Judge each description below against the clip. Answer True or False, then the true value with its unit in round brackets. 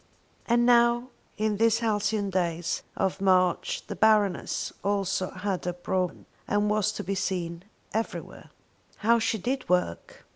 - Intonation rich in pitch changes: False (3.2 semitones)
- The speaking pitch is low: False (205 Hz)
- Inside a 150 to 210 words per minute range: False (140 wpm)